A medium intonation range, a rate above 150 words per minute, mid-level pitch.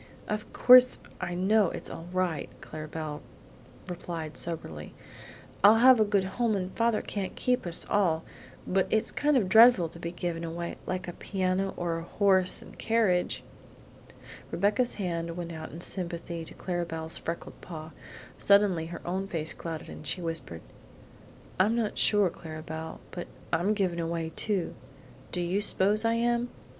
Yes: average, 3.8 semitones; average, 160 wpm; medium, 180 Hz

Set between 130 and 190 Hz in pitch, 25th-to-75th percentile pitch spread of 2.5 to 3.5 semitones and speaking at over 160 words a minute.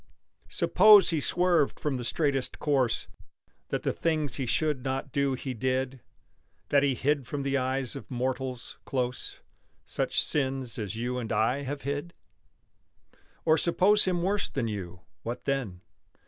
No: low, 135 Hz; average, 2.9 semitones; average, 150 wpm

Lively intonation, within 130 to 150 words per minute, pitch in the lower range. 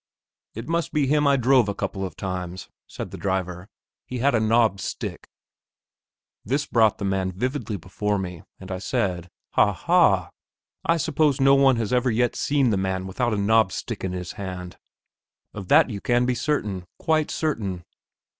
No: wide, 5.8 semitones; average, 180 wpm; low, 110 Hz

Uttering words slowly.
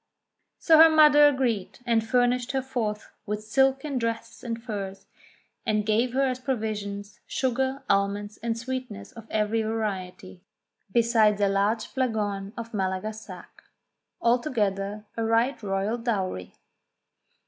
Yes: slow, 130 wpm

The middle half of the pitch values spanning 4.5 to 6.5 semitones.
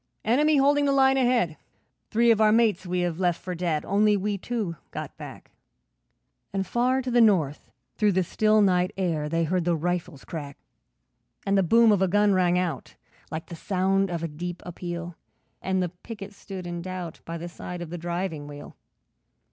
No: average, 3.6 semitones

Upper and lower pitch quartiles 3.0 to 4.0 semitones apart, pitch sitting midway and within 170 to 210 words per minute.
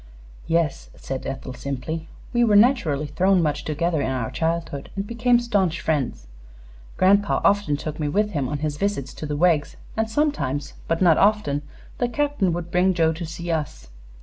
No: wide, 5.6 semitones; medium, 165 Hz; average, 175 wpm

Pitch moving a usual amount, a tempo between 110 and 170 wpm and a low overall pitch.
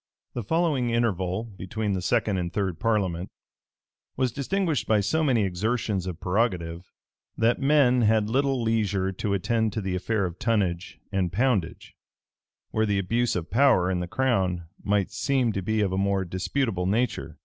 Yes: average, 4.3 semitones; average, 165 wpm; low, 105 Hz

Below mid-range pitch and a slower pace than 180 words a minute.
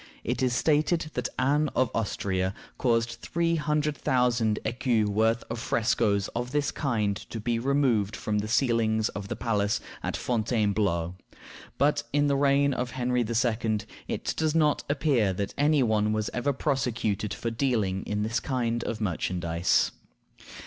Yes: low, 115 Hz; average, 155 wpm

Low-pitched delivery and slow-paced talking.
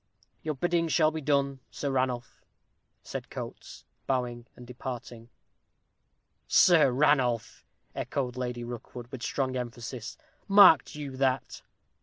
Yes: low, 130 Hz; slow, 115 wpm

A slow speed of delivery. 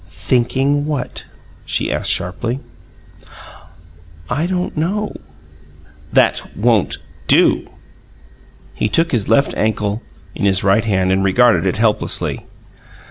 Yes: slow, 110 wpm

